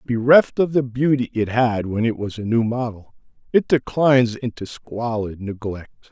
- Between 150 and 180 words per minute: Yes, average, 165 wpm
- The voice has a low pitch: Yes, low, 120 Hz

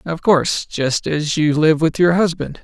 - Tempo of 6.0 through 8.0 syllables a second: No, 4.4 syllables/s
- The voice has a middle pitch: Yes, medium, 160 Hz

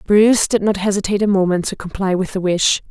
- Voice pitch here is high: Yes, high, 195 Hz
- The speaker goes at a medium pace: No, fast, 225 wpm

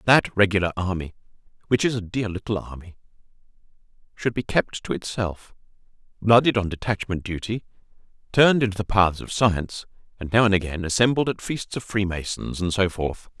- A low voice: Yes, low, 100 Hz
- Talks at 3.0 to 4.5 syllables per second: No, 5.5 syllables/s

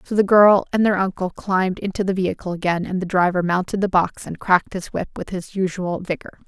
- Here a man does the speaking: No, female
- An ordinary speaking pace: No, fast, 230 wpm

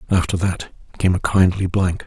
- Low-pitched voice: Yes, very low, 90 Hz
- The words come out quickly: No, average, 175 wpm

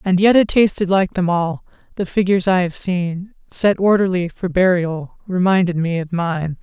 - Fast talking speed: No, average, 180 wpm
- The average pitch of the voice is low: No, medium, 185 Hz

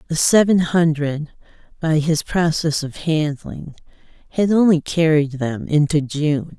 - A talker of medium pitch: Yes, medium, 155 Hz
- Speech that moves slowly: Yes, slow, 130 wpm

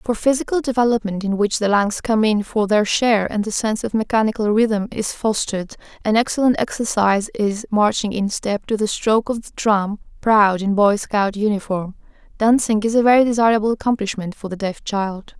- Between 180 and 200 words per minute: Yes, average, 185 wpm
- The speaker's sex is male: No, female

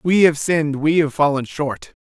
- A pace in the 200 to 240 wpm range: Yes, fast, 205 wpm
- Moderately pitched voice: Yes, medium, 150 Hz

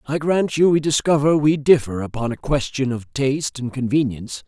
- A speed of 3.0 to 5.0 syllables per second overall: No, 5.3 syllables/s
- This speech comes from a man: Yes, male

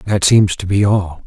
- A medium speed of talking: No, fast, 235 wpm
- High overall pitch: No, very low, 95 Hz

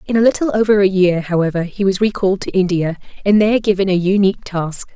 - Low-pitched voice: No, high, 195 Hz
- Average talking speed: No, fast, 220 wpm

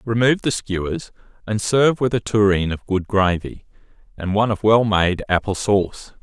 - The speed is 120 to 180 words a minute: Yes, average, 175 wpm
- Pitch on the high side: No, low, 105 Hz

